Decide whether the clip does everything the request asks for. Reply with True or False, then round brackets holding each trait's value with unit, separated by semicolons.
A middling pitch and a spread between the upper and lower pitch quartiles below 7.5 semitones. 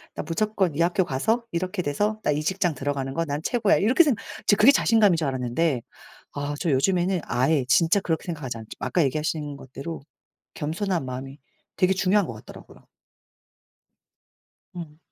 True (165 Hz; 5.3 semitones)